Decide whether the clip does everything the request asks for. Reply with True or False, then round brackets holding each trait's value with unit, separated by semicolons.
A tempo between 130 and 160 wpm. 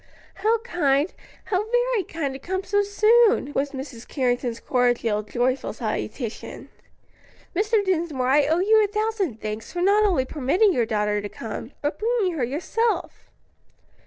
True (150 wpm)